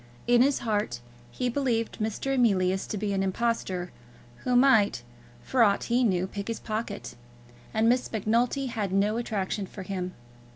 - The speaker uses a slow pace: No, average, 160 wpm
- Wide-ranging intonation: No, average, 3.7 semitones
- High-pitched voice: Yes, high, 215 Hz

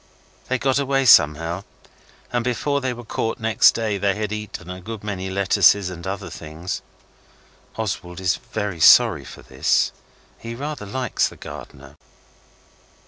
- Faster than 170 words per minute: No, average, 145 wpm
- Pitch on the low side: Yes, low, 100 Hz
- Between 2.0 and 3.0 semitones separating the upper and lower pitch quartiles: No, average, 4.4 semitones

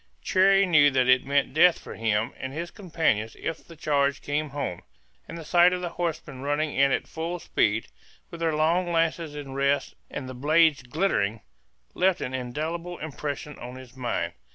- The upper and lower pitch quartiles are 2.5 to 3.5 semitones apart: No, average, 4.2 semitones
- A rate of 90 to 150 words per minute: No, average, 180 wpm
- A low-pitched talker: No, medium, 150 Hz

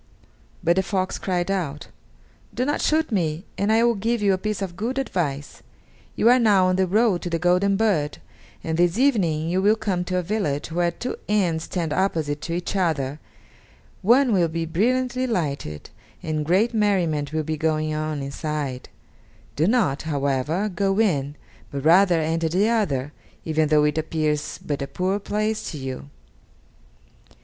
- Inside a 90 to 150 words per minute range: No, average, 175 wpm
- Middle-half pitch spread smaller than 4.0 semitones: No, average, 5.0 semitones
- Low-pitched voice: No, medium, 175 Hz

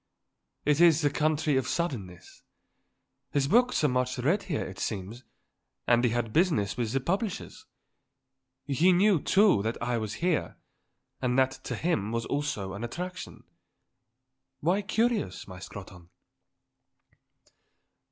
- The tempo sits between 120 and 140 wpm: Yes, slow, 135 wpm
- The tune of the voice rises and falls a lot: Yes, wide, 7.3 semitones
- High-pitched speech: No, low, 135 Hz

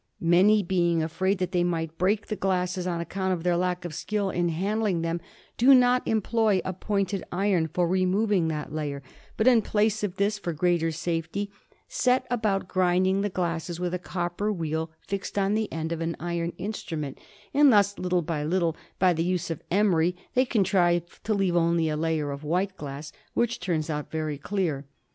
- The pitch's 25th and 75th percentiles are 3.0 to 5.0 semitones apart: Yes, average, 3.4 semitones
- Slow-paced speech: No, average, 190 wpm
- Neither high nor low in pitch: Yes, medium, 180 Hz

